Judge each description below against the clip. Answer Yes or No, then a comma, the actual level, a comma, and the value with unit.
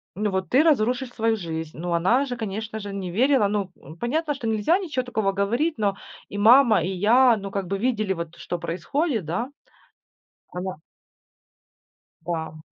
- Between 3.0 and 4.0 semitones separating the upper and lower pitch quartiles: No, average, 5.0 semitones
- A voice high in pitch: Yes, high, 210 Hz